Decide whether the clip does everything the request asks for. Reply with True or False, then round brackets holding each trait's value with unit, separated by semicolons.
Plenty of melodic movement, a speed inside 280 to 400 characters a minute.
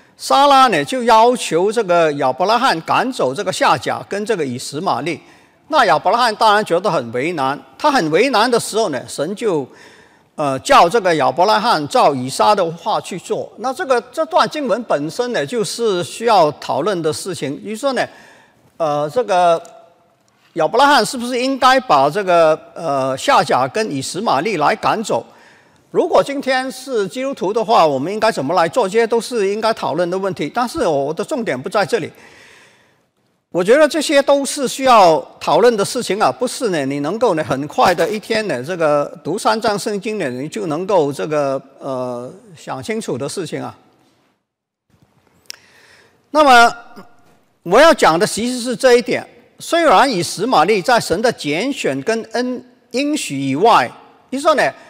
False (7.3 semitones; 250 characters per minute)